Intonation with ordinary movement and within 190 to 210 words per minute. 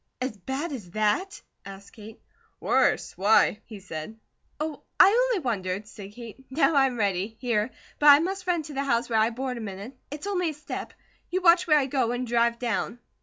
No: wide, 6.0 semitones; fast, 205 wpm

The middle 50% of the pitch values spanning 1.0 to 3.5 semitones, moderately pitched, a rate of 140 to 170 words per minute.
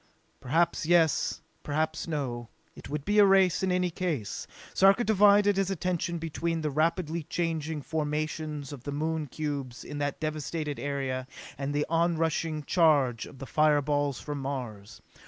Yes: average, 2.9 semitones; medium, 155 Hz; average, 155 wpm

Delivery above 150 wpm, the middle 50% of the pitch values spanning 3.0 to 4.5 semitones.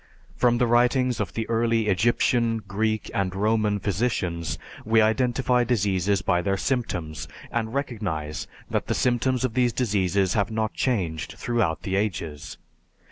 No: average, 140 wpm; average, 3.9 semitones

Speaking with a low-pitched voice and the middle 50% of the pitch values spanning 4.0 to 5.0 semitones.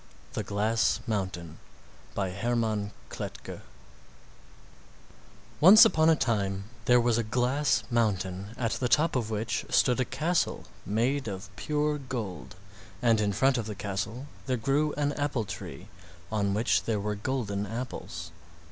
Yes: low, 115 Hz; average, 4.4 semitones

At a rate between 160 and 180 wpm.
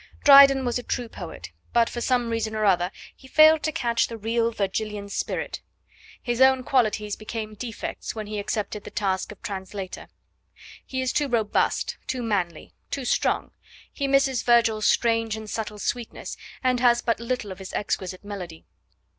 Yes: average, 170 wpm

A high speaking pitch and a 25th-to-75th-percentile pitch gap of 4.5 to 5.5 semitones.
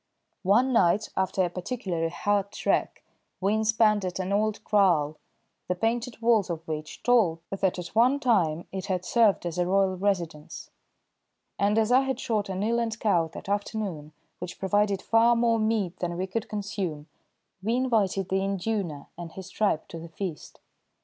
No: high, 195 Hz; average, 3.7 semitones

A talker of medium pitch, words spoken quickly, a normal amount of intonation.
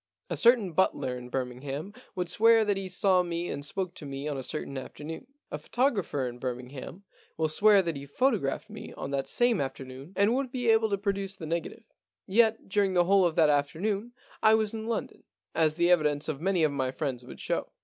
No: medium, 175 Hz; fast, 215 wpm; wide, 6.5 semitones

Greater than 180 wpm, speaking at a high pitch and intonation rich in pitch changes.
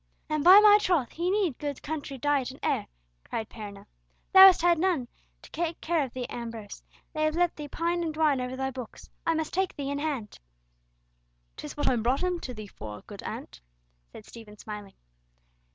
Yes: average, 200 wpm; very high, 290 Hz; wide, 6.1 semitones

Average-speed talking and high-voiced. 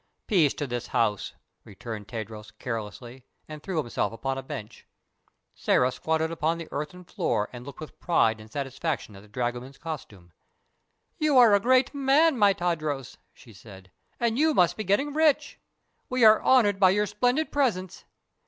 No: average, 165 wpm; medium, 155 Hz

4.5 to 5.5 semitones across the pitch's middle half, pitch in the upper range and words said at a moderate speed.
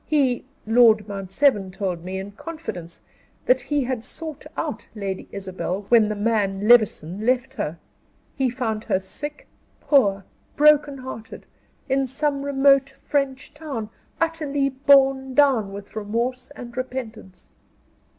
No: average, 5.2 semitones; high, 245 Hz; slow, 130 wpm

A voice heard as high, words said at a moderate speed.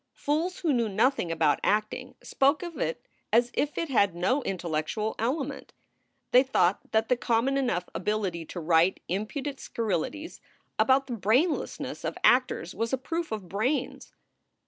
Yes: high, 230 Hz; average, 150 wpm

